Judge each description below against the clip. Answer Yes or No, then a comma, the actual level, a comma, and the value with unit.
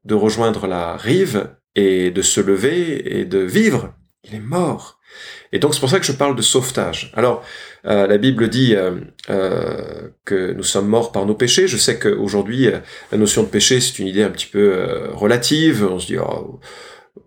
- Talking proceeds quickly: No, average, 200 wpm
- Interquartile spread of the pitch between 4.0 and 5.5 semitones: Yes, average, 5.2 semitones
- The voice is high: No, low, 110 Hz